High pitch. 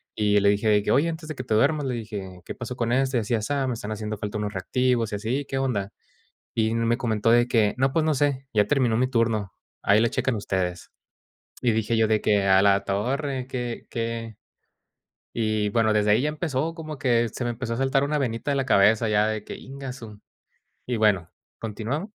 No: low, 115 Hz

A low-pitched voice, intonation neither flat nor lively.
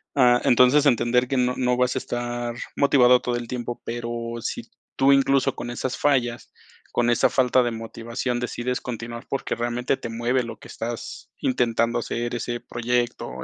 No: low, 120 Hz; narrow, 1.1 semitones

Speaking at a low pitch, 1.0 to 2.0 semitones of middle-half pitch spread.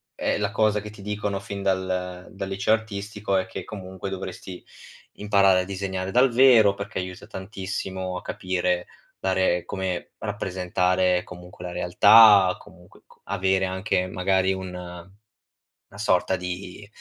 Yes: very low, 95 Hz; narrow, 1.7 semitones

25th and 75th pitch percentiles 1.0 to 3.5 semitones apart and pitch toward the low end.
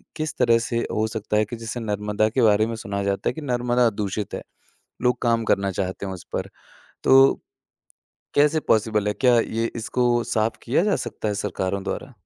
Yes: average, 2.8 semitones; low, 110 Hz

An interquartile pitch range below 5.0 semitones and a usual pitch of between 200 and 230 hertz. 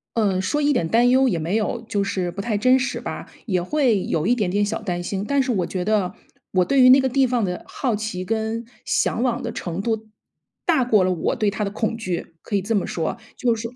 Yes: average, 4.6 semitones; high, 215 Hz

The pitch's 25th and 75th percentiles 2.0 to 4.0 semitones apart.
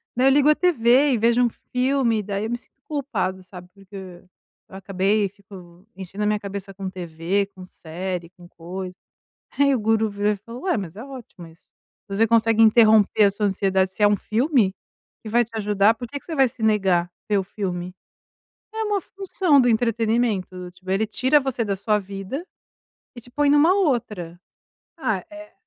No: average, 4.5 semitones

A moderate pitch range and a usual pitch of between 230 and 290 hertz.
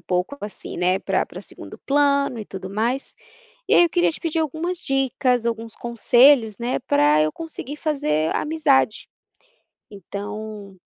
No: wide, 6.1 semitones; high, 235 Hz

